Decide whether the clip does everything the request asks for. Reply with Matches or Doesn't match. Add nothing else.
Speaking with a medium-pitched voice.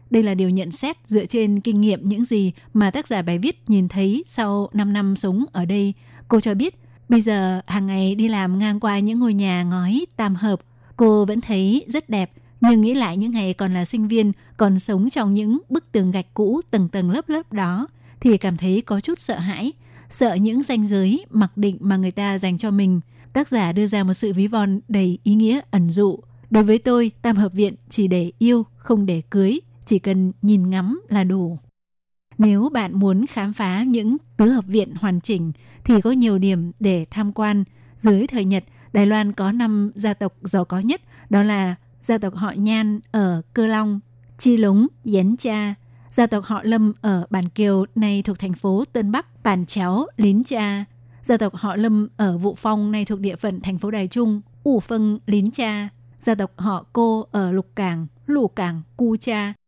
Doesn't match